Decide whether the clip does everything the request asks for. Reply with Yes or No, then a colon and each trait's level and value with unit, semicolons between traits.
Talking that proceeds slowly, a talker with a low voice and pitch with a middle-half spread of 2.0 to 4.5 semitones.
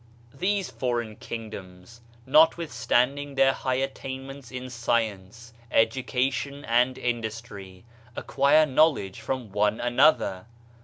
Yes: slow, 100 wpm; low, 125 Hz; average, 3.4 semitones